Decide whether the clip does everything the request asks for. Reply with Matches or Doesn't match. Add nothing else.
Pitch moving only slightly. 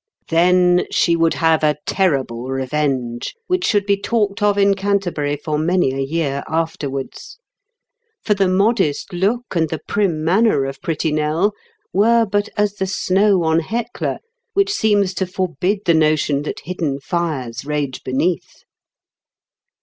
Doesn't match